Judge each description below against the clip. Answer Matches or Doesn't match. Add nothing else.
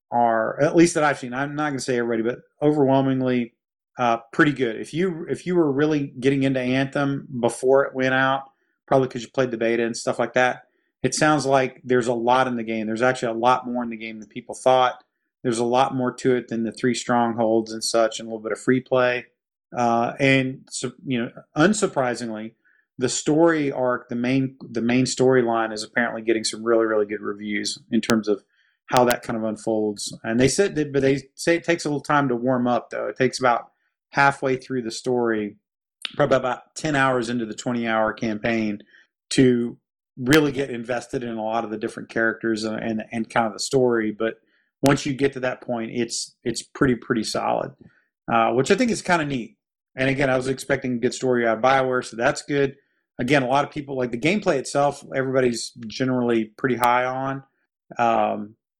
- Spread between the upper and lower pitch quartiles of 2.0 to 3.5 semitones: Matches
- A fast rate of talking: Matches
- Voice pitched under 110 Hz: Doesn't match